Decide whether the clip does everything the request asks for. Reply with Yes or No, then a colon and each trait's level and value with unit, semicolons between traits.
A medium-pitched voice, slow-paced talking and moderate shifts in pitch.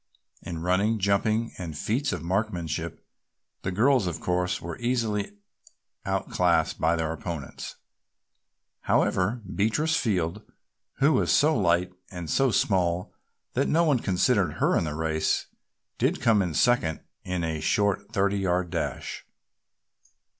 No: very low, 95 Hz; slow, 130 wpm; average, 4.6 semitones